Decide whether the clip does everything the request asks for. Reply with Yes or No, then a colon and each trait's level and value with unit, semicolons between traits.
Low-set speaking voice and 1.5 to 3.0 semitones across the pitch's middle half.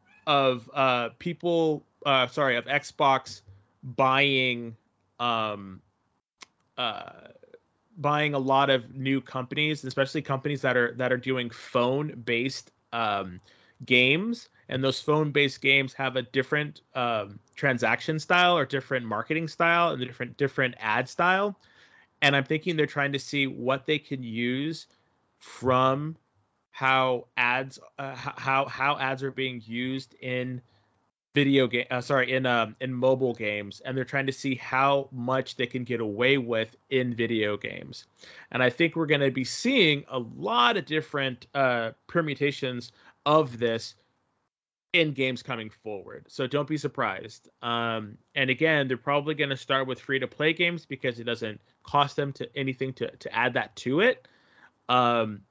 Yes: low, 130 Hz; narrow, 2.6 semitones